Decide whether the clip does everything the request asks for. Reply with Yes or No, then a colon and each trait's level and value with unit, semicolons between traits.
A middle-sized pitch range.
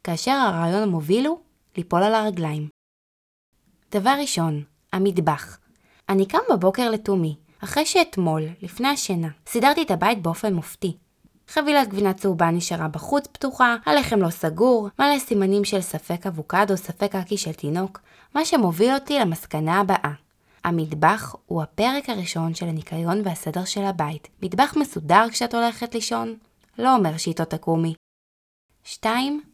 No: wide, 6.2 semitones